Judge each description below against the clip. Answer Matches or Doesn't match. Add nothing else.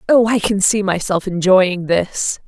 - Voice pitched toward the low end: Doesn't match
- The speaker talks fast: Doesn't match